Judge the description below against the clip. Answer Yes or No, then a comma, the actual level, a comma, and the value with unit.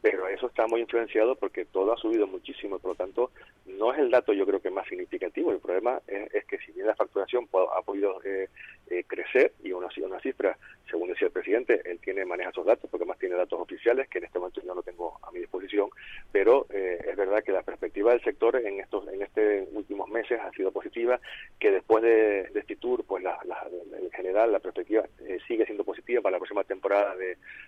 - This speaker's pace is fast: Yes, fast, 230 wpm